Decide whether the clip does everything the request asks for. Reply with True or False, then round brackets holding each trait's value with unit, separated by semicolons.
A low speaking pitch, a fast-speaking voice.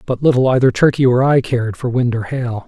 True (125 Hz; 245 wpm)